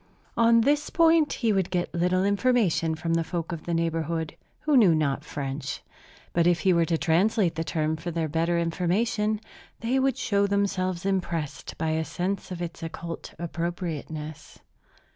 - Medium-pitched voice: Yes, medium, 175 Hz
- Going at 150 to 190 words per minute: Yes, average, 165 wpm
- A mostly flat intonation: No, average, 3.7 semitones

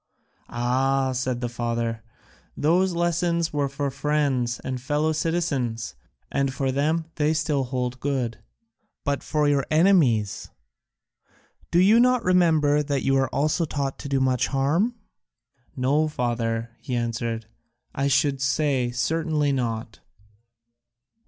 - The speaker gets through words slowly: Yes, slow, 125 wpm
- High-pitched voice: No, medium, 140 Hz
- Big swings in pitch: No, average, 3.8 semitones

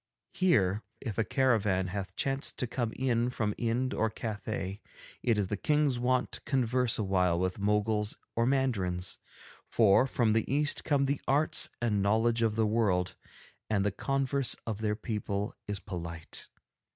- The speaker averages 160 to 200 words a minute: Yes, average, 165 wpm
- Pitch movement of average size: Yes, average, 4.1 semitones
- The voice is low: Yes, low, 110 Hz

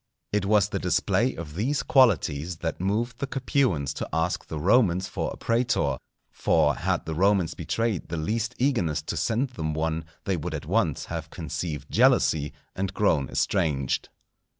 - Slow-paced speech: No, average, 165 wpm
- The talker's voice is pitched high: No, very low, 90 Hz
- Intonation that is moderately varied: No, wide, 6.5 semitones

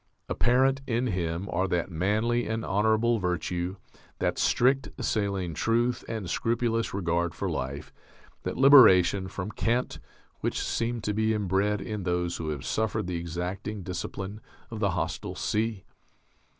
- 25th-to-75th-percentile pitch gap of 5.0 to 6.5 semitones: No, average, 4.3 semitones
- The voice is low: Yes, low, 100 Hz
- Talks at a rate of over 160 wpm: No, average, 140 wpm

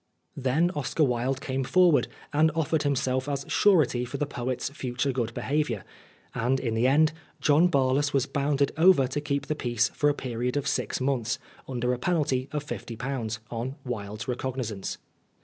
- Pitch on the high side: No, low, 135 Hz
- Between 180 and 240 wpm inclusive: No, average, 165 wpm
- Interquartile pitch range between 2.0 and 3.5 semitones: Yes, average, 2.9 semitones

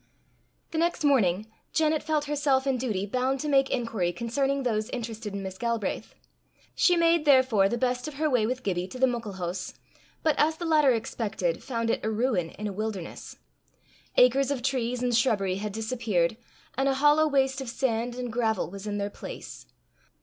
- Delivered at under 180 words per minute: No, average, 185 wpm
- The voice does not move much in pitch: No, average, 4.4 semitones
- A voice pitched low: No, high, 245 Hz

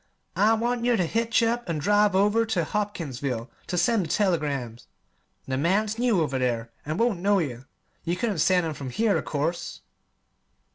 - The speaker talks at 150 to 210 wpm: Yes, average, 180 wpm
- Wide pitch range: Yes, wide, 6.8 semitones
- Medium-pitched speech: Yes, medium, 180 Hz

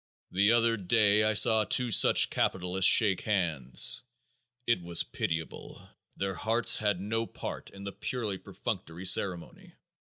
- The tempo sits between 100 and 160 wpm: Yes, average, 140 wpm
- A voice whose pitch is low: Yes, low, 100 Hz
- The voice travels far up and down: No, average, 3.6 semitones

